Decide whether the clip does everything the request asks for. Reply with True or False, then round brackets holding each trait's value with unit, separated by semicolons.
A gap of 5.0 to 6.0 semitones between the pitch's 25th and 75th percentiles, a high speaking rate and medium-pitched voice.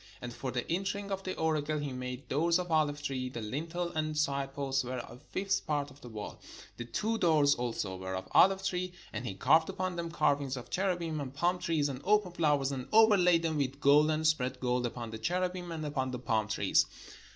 True (5.3 semitones; 220 wpm; 145 Hz)